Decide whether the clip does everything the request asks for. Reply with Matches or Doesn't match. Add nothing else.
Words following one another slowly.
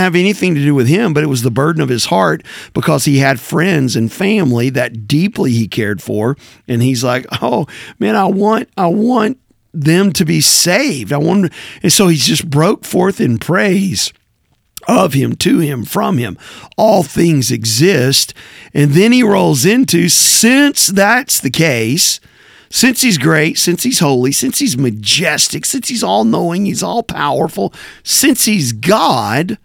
Doesn't match